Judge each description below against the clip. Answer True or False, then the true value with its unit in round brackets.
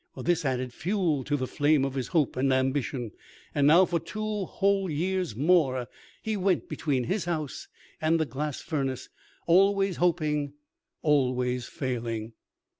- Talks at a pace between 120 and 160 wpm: True (145 wpm)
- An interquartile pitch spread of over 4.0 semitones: True (5.2 semitones)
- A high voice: False (150 Hz)